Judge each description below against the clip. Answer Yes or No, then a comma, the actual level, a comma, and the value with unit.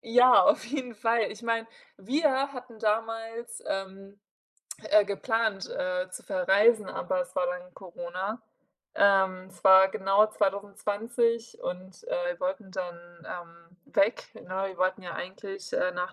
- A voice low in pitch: No, high, 200 Hz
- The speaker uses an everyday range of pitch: Yes, average, 3.7 semitones